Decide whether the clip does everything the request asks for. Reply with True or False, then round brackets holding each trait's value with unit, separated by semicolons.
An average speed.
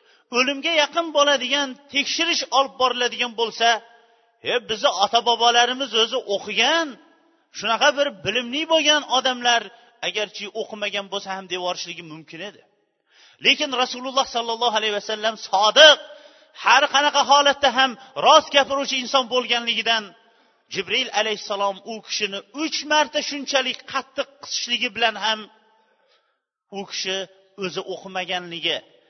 False (110 wpm)